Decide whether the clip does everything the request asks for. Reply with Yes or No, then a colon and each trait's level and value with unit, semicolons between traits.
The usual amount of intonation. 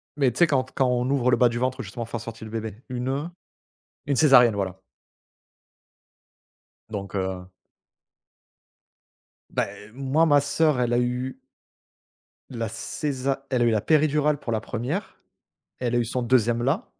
Yes: average, 3.2 semitones